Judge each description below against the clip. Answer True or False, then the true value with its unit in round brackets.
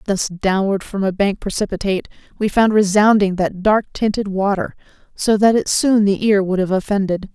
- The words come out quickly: False (180 wpm)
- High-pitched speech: True (200 Hz)